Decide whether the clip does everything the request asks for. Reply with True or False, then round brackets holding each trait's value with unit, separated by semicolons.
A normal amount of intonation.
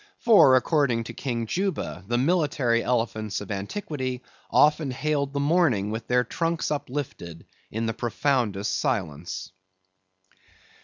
True (4.9 semitones)